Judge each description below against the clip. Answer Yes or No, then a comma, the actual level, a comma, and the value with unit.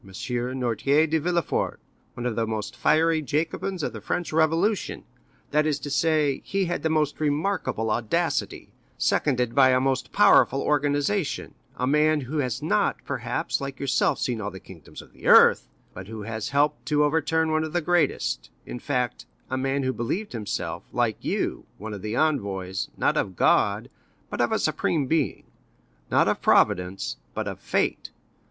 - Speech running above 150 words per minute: Yes, average, 170 wpm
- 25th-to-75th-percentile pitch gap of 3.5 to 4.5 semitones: No, average, 4.9 semitones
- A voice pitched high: No, medium, 140 Hz